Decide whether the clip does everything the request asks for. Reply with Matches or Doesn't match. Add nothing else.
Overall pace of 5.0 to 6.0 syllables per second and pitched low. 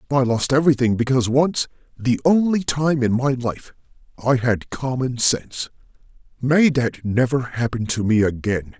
Doesn't match